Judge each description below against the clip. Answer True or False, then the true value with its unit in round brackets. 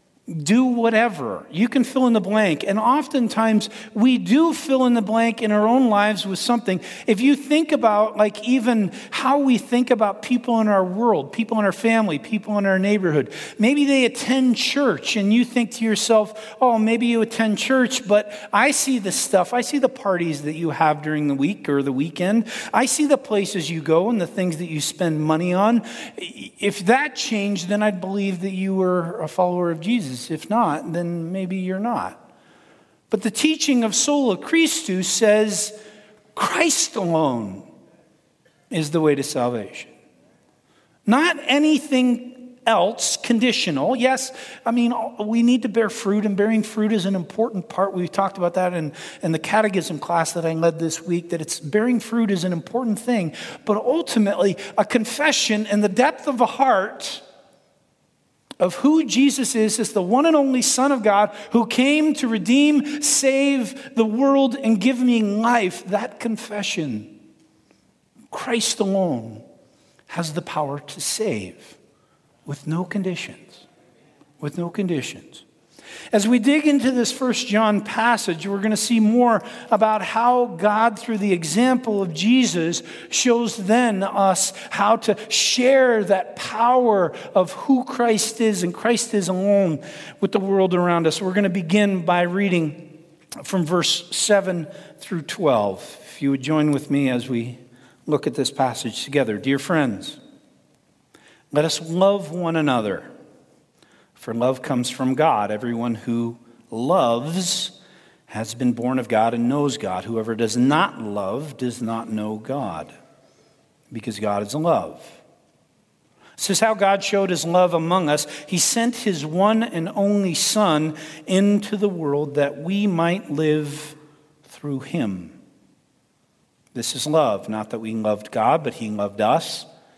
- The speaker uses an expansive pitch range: True (6.2 semitones)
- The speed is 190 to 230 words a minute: False (160 wpm)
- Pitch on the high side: True (205 Hz)